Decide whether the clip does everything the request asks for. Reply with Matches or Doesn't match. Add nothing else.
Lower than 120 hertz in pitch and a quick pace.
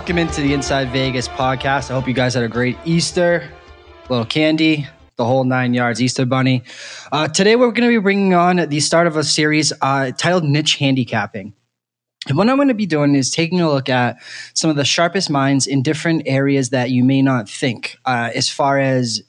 Doesn't match